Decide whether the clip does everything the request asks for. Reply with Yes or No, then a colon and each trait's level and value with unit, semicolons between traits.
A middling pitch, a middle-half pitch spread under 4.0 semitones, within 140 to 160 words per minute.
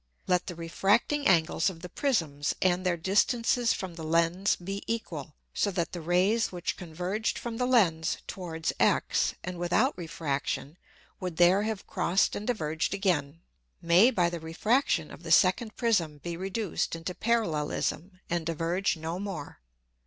Yes: medium, 180 Hz; average, 3.6 semitones; average, 155 wpm